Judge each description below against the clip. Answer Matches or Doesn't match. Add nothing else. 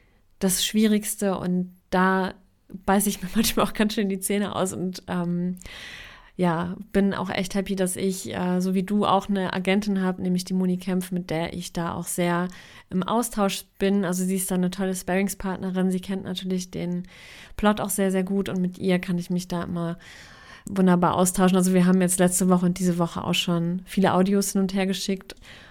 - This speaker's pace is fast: Matches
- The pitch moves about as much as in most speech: Doesn't match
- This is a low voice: Doesn't match